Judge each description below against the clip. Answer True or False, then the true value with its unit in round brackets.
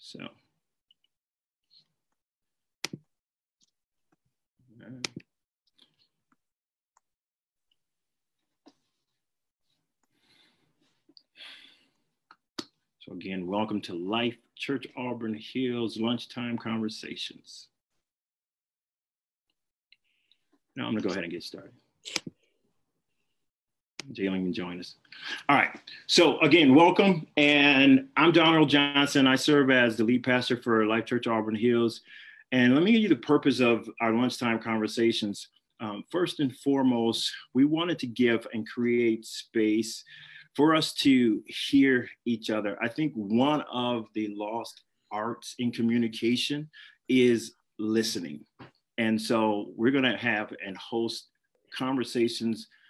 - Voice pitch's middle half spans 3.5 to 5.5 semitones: False (3.0 semitones)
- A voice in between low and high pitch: False (120 Hz)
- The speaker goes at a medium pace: False (105 wpm)